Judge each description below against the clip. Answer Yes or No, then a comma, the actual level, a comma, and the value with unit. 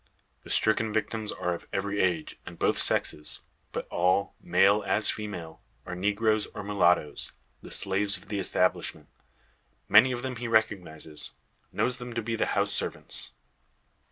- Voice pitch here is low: Yes, low, 105 Hz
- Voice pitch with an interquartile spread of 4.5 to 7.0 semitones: No, average, 3.5 semitones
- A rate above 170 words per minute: No, average, 155 wpm